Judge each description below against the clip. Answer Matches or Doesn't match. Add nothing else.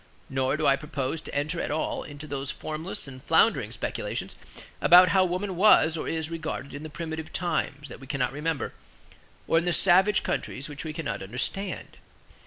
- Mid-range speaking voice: Matches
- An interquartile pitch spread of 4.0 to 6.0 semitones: Doesn't match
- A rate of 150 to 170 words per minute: Doesn't match